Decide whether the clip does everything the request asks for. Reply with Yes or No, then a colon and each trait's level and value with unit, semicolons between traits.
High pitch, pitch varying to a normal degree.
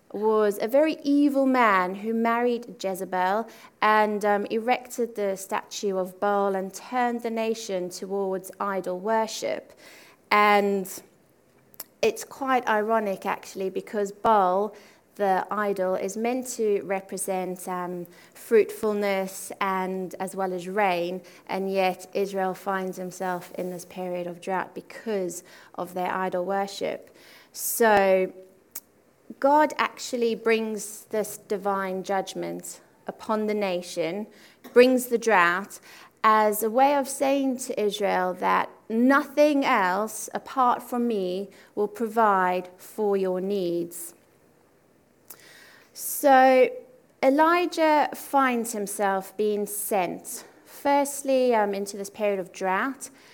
Yes: high, 205 Hz; average, 3.7 semitones